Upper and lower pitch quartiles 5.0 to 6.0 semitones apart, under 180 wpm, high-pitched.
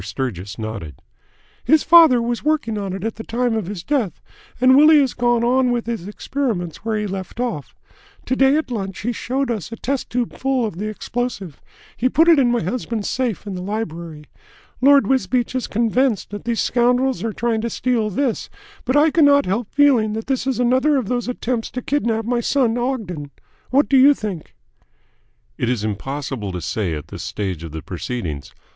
No: wide, 5.5 semitones; average, 195 wpm; high, 235 Hz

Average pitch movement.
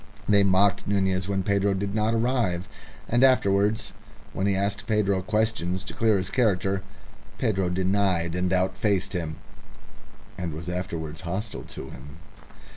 No: narrow, 2.3 semitones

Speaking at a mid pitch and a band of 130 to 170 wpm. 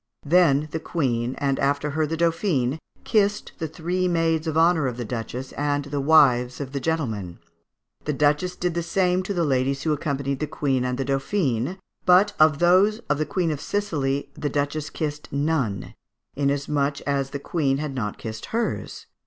No: medium, 145 Hz; average, 180 wpm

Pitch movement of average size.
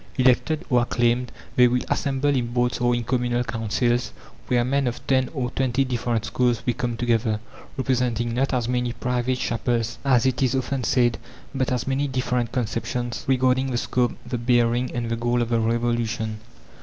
No: narrow, 1.4 semitones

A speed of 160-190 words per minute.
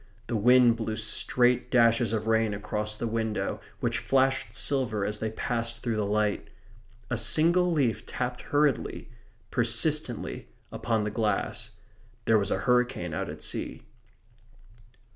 No: average, 140 wpm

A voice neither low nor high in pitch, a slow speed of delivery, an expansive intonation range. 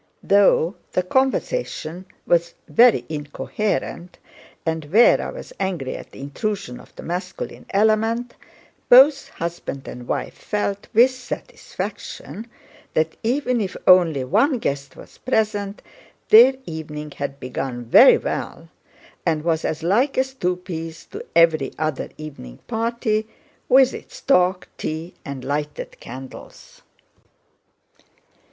Yes: medium, 180 Hz; slow, 120 wpm; wide, 6.9 semitones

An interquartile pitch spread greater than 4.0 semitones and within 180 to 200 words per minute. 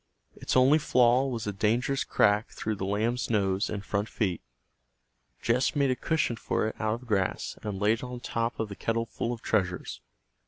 No: average, 3.2 semitones; average, 195 wpm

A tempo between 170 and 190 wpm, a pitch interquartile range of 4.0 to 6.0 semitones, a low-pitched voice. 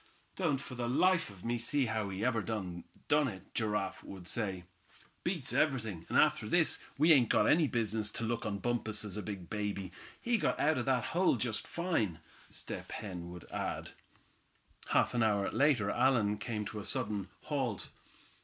Yes: average, 180 wpm; average, 4.5 semitones; low, 110 Hz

